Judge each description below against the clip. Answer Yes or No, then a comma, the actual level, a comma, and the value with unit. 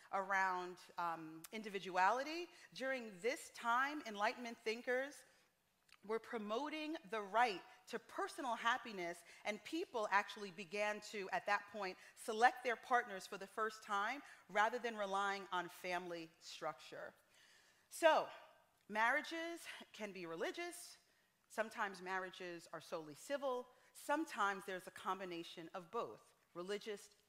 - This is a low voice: No, high, 215 Hz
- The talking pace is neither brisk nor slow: No, slow, 115 wpm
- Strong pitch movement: No, average, 4.8 semitones